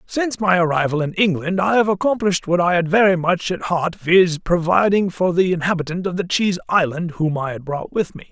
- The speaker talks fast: Yes, fast, 215 wpm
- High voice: No, medium, 180 Hz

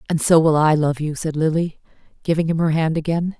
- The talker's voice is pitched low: No, medium, 160 Hz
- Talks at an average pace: No, fast, 230 wpm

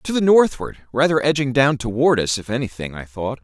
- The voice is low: Yes, low, 130 Hz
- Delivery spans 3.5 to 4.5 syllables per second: No, 5.5 syllables/s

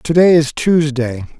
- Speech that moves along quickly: No, average, 170 wpm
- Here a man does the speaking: Yes, male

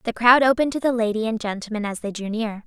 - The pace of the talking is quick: Yes, fast, 270 wpm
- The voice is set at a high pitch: Yes, high, 225 Hz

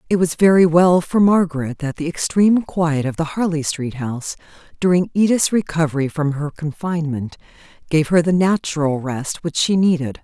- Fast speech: No, average, 170 wpm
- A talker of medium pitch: Yes, medium, 160 Hz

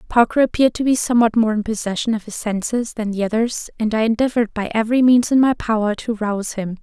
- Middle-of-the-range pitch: No, high, 225 Hz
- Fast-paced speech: Yes, fast, 230 wpm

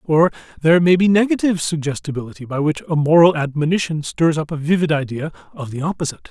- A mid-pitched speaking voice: Yes, medium, 160 Hz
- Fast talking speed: No, average, 180 wpm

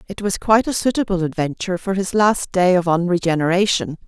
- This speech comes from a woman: Yes, female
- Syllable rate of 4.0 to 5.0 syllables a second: No, 5.9 syllables/s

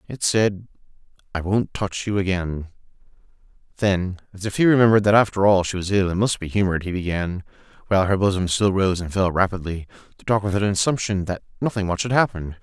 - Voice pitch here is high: No, very low, 95 Hz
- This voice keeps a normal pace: Yes, average, 195 wpm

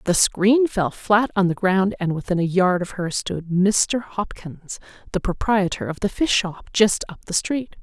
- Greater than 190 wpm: Yes, average, 200 wpm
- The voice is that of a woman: Yes, female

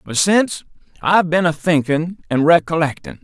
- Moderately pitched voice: Yes, medium, 165 Hz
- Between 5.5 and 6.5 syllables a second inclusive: No, 5.1 syllables/s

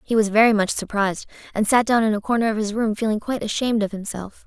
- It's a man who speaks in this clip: No, female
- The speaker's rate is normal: No, fast, 255 wpm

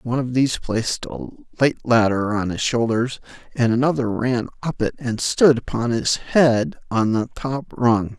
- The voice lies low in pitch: Yes, low, 120 Hz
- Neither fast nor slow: Yes, average, 175 wpm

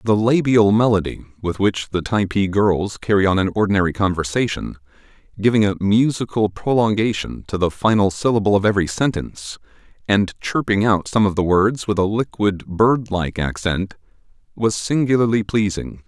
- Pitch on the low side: Yes, low, 100 Hz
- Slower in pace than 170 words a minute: Yes, average, 150 wpm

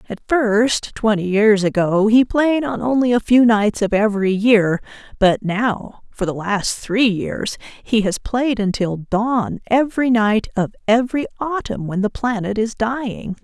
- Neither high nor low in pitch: No, high, 220 Hz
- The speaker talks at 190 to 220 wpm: No, average, 165 wpm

